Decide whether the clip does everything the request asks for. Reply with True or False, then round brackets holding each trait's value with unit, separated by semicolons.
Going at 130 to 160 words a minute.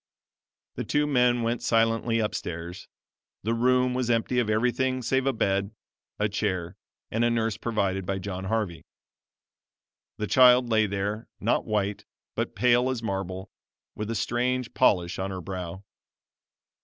True (150 wpm)